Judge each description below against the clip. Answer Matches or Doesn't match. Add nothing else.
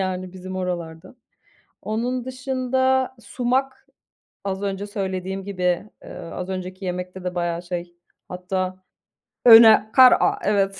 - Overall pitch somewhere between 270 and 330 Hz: Doesn't match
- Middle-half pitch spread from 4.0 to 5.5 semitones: Matches